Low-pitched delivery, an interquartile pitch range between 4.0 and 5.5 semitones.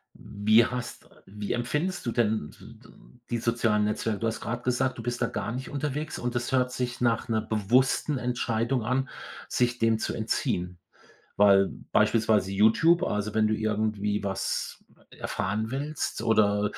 No: low, 115 Hz; average, 2.8 semitones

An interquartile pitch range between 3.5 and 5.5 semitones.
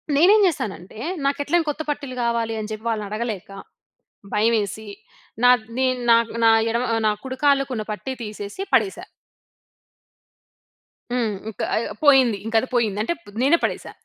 Yes: average, 4.2 semitones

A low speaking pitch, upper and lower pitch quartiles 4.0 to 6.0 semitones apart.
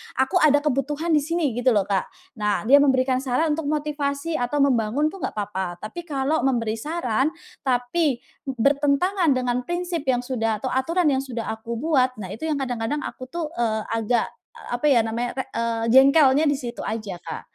No: very high, 265 Hz; average, 4.3 semitones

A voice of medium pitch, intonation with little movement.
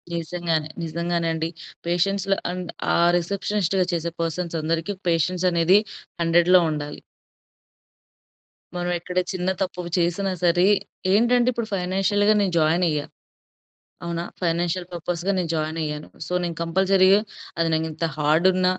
Yes: medium, 175 Hz; narrow, 2.0 semitones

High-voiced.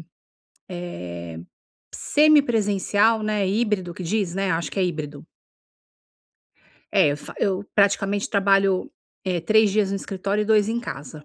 Yes: high, 200 Hz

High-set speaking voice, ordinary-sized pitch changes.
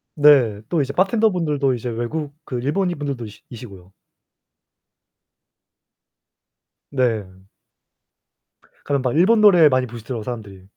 No: low, 130 Hz; average, 5.0 semitones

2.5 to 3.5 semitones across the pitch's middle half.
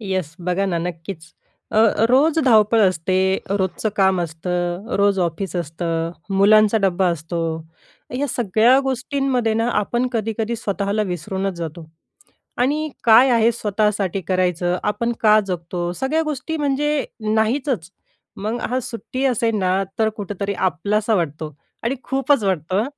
No: average, 4.8 semitones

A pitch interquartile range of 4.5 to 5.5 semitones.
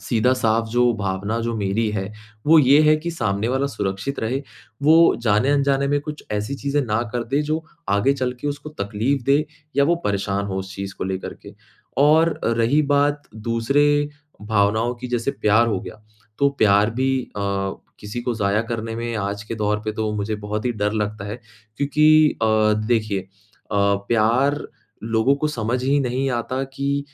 Yes: average, 4.9 semitones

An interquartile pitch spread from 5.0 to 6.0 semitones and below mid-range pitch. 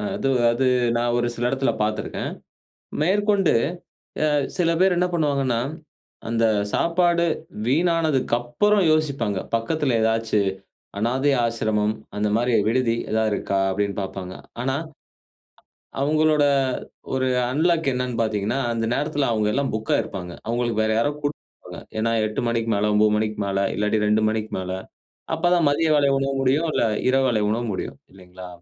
Yes: average, 5.3 semitones; low, 120 Hz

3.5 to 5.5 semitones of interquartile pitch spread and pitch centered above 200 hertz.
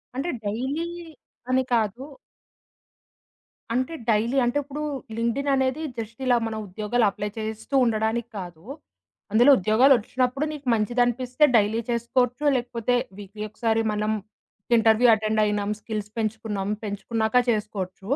No: average, 2.9 semitones; high, 225 Hz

